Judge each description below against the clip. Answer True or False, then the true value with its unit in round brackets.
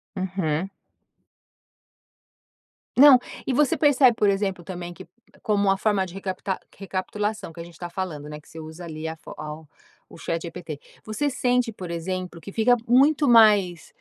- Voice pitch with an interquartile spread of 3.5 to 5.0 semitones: True (4.4 semitones)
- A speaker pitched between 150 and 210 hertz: True (190 Hz)